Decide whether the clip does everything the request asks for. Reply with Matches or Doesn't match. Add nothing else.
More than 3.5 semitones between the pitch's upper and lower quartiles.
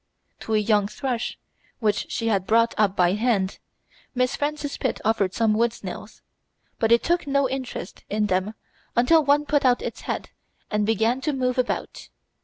Matches